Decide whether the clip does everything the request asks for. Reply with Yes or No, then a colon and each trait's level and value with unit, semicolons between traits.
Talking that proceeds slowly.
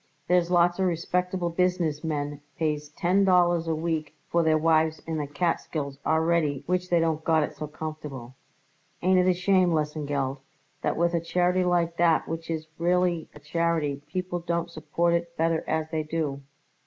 No: average, 175 wpm